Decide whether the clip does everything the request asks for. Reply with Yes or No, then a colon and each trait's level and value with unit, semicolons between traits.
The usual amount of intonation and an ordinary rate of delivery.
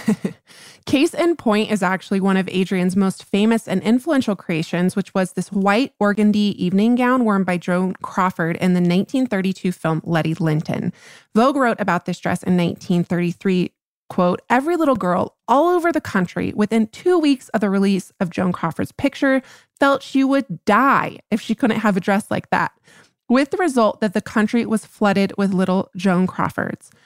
Yes: average, 4.5 semitones; average, 175 wpm